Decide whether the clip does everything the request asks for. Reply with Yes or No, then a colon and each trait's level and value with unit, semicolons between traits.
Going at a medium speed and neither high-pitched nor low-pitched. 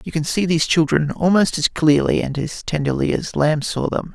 No: fast, 215 wpm; medium, 155 Hz